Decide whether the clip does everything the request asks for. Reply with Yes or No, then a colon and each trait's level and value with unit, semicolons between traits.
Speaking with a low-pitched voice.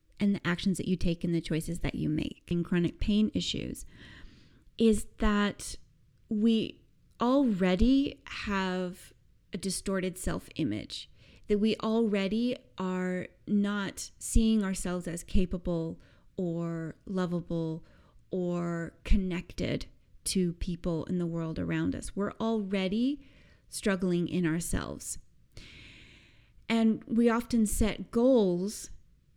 No: medium, 185 Hz